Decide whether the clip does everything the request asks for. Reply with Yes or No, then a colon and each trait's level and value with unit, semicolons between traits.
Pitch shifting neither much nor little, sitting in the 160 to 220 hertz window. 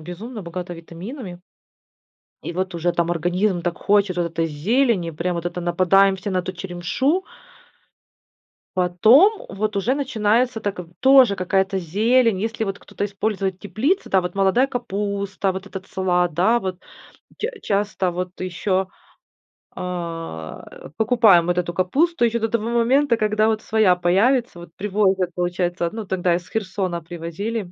Yes: average, 3.8 semitones; high, 190 Hz